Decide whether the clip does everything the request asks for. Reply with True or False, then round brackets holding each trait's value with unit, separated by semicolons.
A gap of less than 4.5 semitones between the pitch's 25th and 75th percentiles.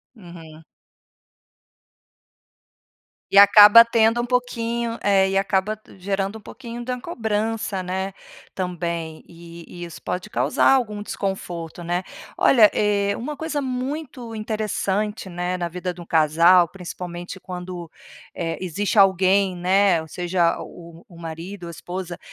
True (3.7 semitones)